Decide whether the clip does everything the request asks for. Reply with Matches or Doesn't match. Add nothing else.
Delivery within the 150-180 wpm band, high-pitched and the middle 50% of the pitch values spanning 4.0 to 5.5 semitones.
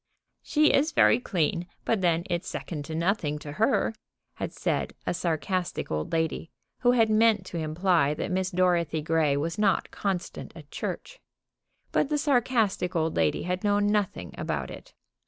Doesn't match